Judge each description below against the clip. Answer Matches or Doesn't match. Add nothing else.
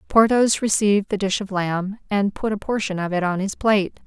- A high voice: Matches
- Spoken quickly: Matches